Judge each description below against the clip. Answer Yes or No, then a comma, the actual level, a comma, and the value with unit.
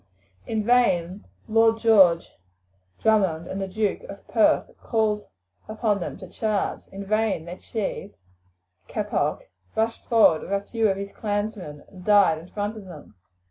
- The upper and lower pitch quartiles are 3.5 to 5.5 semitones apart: No, average, 2.8 semitones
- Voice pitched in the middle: No, high, 205 Hz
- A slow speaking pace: No, average, 150 wpm